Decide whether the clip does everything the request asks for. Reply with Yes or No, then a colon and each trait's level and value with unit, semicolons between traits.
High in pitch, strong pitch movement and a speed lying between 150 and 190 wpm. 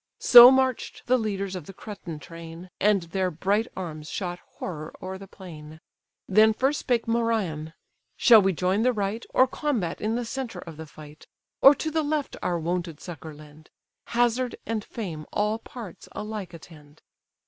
Yes: high, 195 Hz; wide, 5.7 semitones; average, 170 wpm